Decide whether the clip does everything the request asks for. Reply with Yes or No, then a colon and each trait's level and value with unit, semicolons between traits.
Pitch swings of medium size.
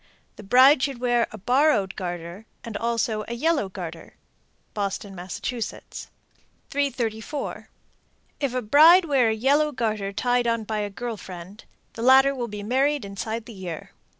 Yes: average, 4.4 semitones